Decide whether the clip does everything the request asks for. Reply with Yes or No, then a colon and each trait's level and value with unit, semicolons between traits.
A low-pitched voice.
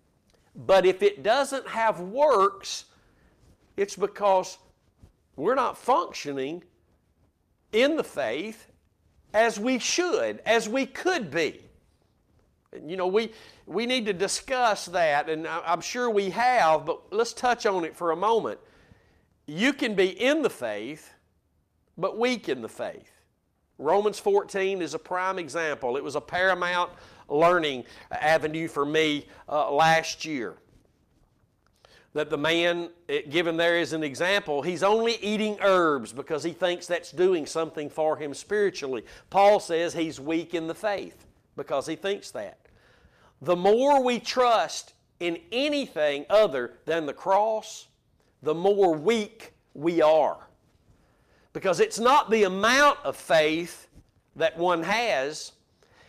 No: high, 190 Hz